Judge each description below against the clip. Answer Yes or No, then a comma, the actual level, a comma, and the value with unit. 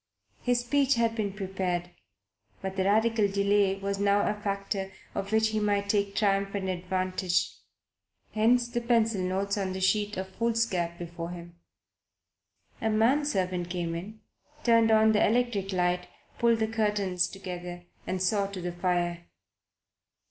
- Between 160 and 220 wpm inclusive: No, average, 150 wpm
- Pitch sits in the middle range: No, high, 200 Hz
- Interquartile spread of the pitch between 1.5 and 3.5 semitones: Yes, average, 3.0 semitones